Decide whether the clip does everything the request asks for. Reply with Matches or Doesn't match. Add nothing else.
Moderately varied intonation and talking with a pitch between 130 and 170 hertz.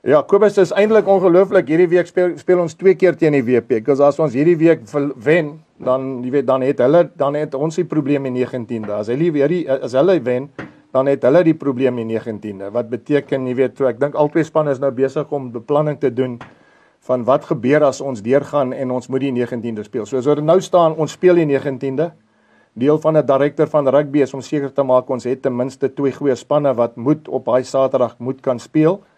Matches